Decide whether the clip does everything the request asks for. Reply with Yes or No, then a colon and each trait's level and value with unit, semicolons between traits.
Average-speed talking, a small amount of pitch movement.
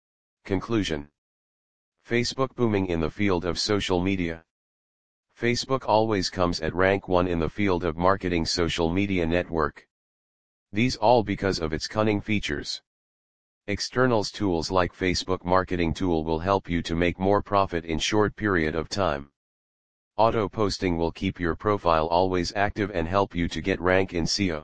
No: average, 155 wpm; average, 3.4 semitones